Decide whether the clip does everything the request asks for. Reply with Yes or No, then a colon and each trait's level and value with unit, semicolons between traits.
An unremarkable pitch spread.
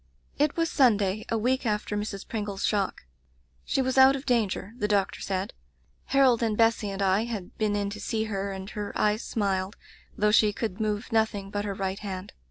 No: narrow, 2.3 semitones